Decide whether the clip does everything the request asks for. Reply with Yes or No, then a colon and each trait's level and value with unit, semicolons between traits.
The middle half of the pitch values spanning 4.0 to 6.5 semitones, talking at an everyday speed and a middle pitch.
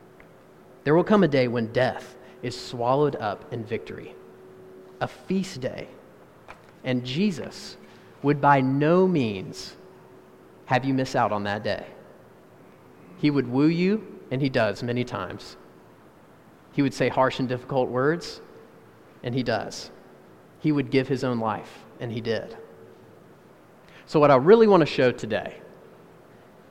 No: average, 4.7 semitones; average, 145 wpm; low, 130 Hz